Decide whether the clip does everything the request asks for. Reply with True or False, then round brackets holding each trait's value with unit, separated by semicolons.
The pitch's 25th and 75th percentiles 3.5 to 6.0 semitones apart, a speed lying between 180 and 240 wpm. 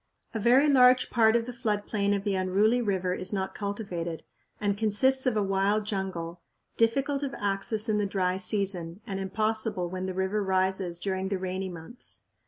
False (2.8 semitones; 185 wpm)